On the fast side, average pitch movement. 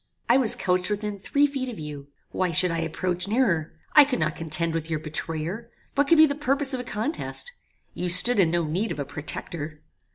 No: fast, 215 wpm; wide, 7.6 semitones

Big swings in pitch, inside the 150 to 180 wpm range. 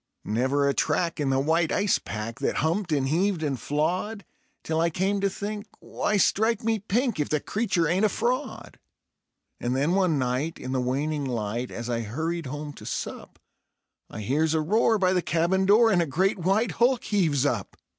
No: wide, 6.2 semitones; average, 195 wpm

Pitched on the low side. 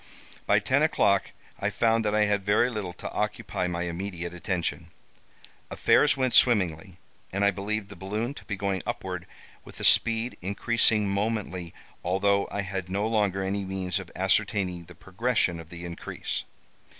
Yes: low, 100 Hz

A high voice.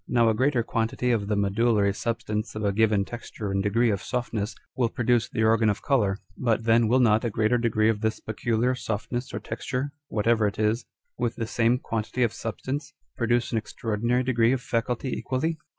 No: low, 115 Hz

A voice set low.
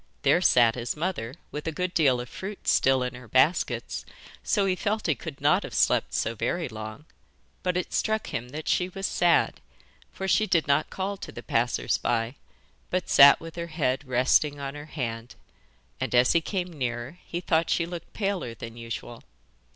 No: medium, 150 Hz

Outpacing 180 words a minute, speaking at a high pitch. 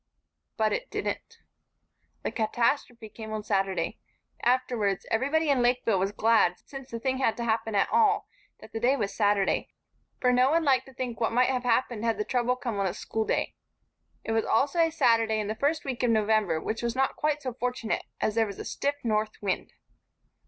Yes: average, 200 wpm; high, 235 Hz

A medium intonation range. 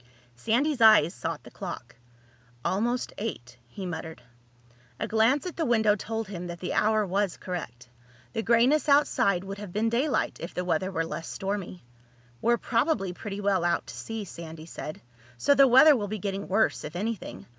Yes: average, 4.7 semitones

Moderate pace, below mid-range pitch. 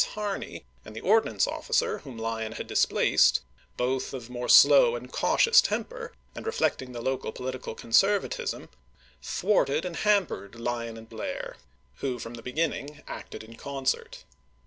Yes: average, 160 wpm; low, 130 Hz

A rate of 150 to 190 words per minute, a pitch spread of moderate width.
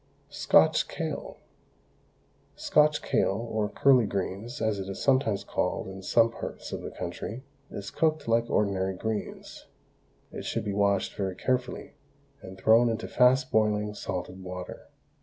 No: average, 140 wpm; average, 3.7 semitones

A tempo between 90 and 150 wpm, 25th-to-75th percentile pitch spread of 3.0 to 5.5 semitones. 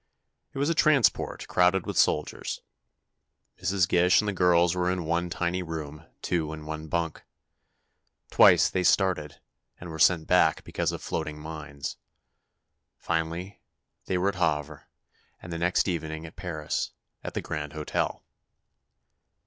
No: average, 140 wpm; narrow, 2.6 semitones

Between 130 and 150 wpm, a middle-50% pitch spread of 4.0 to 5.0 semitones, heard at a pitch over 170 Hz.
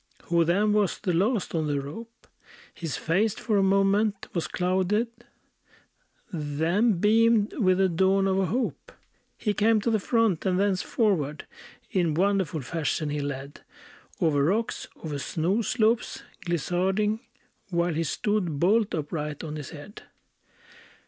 Yes: average, 140 wpm; average, 4.7 semitones; medium, 185 Hz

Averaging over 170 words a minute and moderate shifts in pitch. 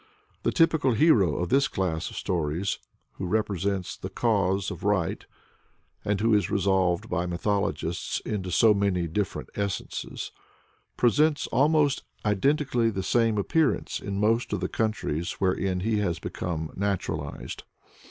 No: slow, 135 wpm; average, 3.9 semitones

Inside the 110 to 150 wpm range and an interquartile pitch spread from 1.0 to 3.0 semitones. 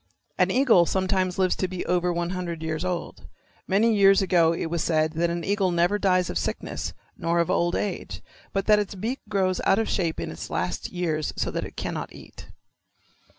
No: average, 200 wpm; narrow, 2.4 semitones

